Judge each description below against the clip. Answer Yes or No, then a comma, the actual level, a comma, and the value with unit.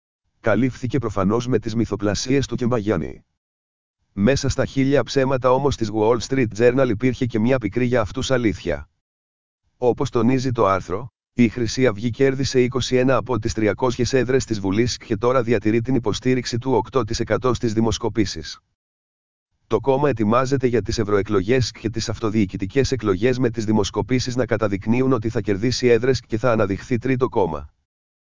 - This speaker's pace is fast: No, average, 150 wpm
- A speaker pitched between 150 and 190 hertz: No, low, 120 Hz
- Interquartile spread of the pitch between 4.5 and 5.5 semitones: No, average, 3.4 semitones